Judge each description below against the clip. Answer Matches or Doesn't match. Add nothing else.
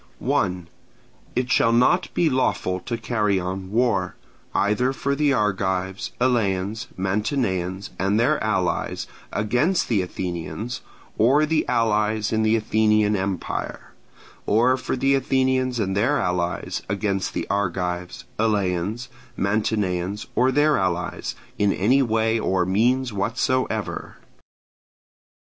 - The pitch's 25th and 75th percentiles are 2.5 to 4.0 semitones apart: Doesn't match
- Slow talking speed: Matches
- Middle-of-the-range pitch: Doesn't match